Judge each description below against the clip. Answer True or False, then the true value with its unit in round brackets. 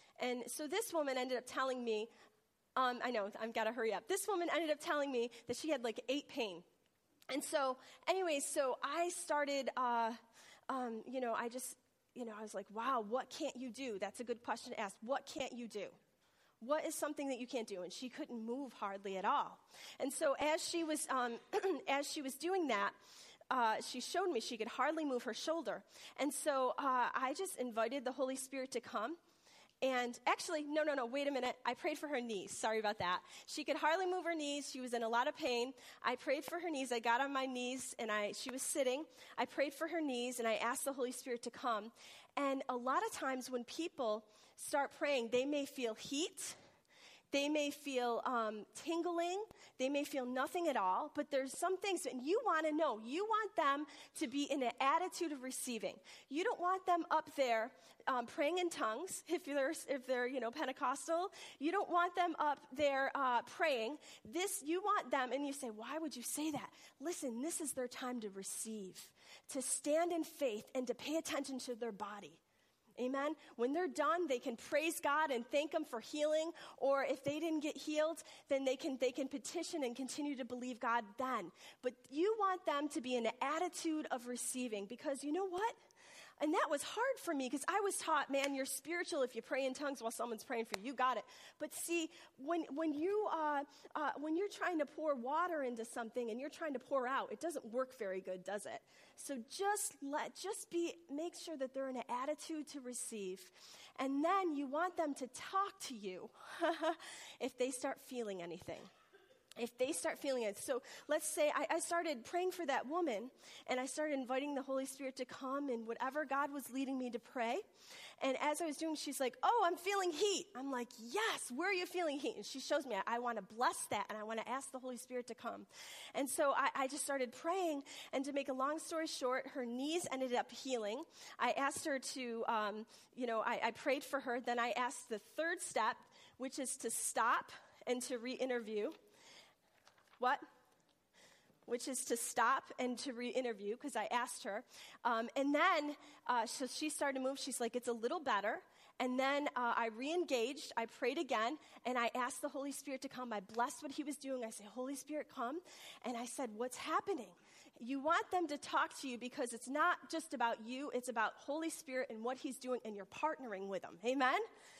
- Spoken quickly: True (215 wpm)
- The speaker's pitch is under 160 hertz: False (270 Hz)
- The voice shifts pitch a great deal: False (4.1 semitones)